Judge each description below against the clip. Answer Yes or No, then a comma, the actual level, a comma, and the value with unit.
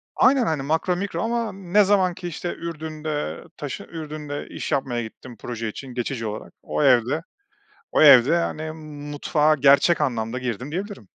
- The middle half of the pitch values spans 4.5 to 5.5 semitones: Yes, average, 5.2 semitones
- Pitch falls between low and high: Yes, medium, 150 Hz